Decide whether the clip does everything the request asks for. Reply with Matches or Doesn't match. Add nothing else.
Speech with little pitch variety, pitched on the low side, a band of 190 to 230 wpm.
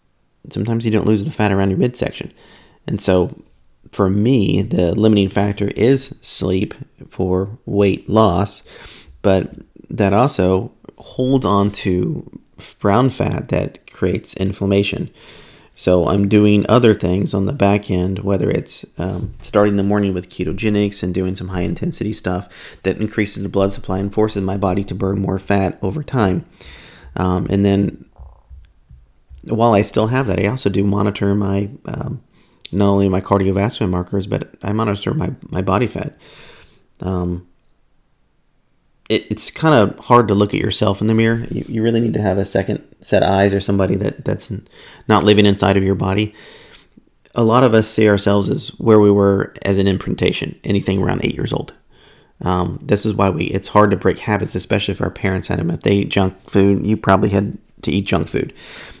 Doesn't match